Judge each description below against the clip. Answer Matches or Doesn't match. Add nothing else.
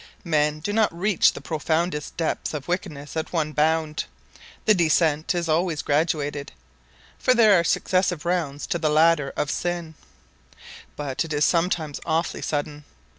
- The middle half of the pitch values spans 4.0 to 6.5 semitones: Doesn't match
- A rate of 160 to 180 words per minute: Doesn't match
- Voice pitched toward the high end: Doesn't match